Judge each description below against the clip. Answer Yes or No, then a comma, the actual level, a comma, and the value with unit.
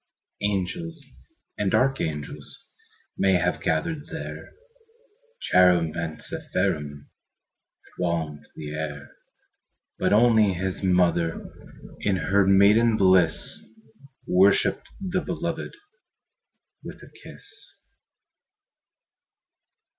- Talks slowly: Yes, slow, 80 wpm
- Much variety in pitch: No, average, 4.8 semitones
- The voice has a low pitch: Yes, very low, 95 Hz